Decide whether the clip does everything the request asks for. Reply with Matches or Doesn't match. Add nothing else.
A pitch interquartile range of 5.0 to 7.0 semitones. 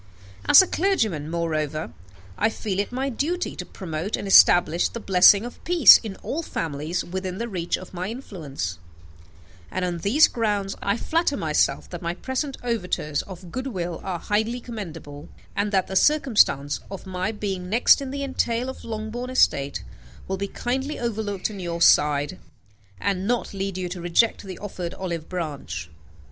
Matches